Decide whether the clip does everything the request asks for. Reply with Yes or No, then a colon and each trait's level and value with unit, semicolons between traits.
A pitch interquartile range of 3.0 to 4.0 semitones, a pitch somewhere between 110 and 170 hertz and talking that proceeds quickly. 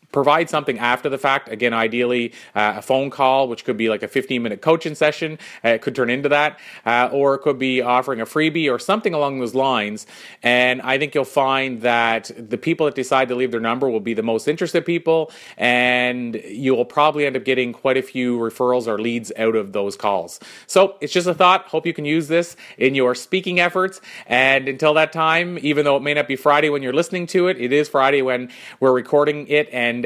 Yes: average, 3.7 semitones; low, 135 Hz; fast, 225 wpm